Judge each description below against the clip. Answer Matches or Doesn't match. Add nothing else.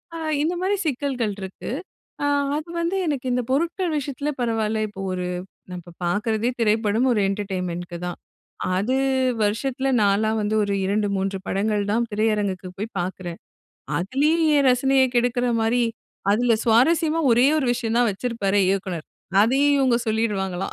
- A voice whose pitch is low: Doesn't match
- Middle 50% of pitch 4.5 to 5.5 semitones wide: Matches